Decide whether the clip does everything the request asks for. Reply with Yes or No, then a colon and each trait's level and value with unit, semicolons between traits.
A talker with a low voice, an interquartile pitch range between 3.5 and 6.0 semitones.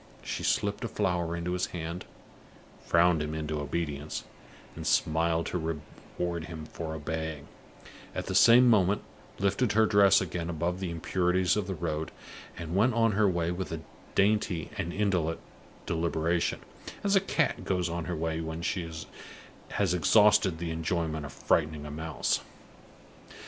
No: very low, 85 Hz; average, 2.9 semitones